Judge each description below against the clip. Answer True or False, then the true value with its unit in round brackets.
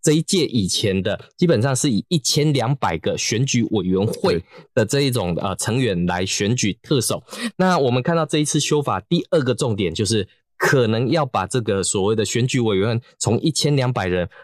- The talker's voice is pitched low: True (125 Hz)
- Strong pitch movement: True (5.9 semitones)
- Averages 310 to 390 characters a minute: False (285 characters per minute)